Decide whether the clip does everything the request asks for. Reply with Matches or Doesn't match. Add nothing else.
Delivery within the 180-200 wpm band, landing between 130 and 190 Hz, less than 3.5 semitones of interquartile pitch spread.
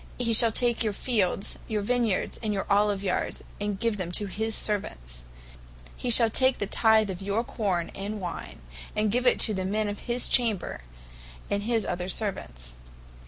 Doesn't match